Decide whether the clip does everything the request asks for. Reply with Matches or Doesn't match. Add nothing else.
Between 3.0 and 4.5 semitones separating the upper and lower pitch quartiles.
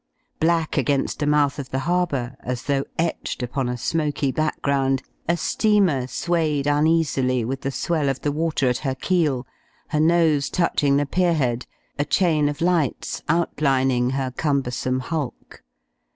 Matches